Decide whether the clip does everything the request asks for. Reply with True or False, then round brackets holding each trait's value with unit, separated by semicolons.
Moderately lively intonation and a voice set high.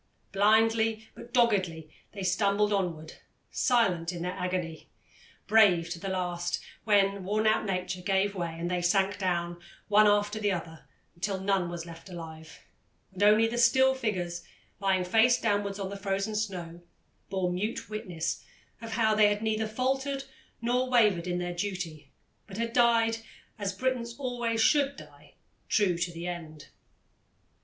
True (3.9 semitones; 200 Hz)